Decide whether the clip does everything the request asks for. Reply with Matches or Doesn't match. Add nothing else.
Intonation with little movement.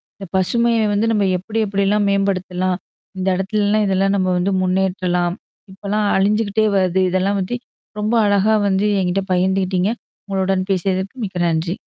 Matches